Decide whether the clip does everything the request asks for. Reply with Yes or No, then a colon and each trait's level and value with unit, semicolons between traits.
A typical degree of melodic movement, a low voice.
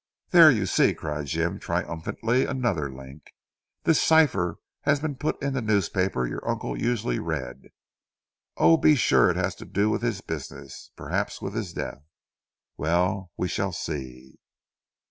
No: wide, 7.8 semitones; very low, 95 Hz